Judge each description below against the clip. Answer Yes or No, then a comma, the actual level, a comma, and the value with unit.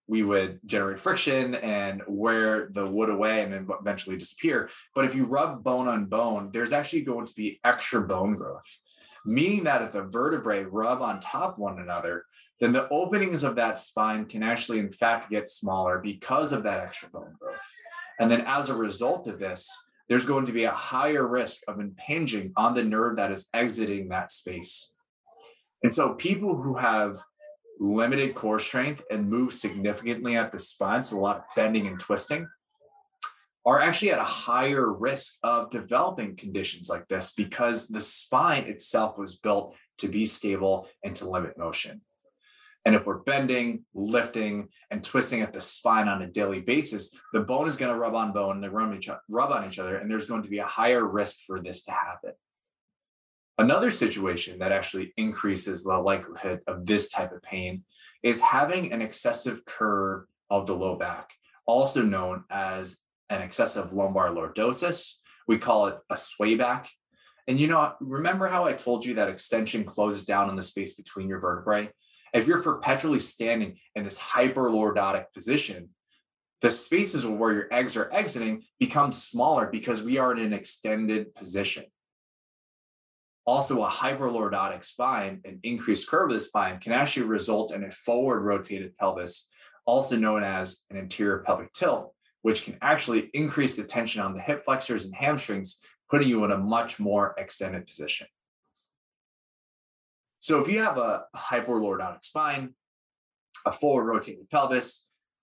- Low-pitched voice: Yes, low, 110 Hz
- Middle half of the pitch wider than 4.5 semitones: Yes, average, 5.0 semitones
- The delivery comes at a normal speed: Yes, average, 170 wpm